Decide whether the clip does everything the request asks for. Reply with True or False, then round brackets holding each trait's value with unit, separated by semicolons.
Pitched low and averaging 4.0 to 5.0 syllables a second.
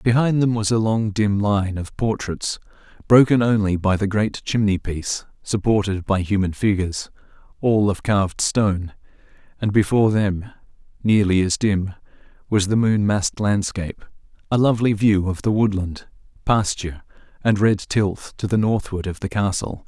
True (105 Hz; 4.8 syllables/s)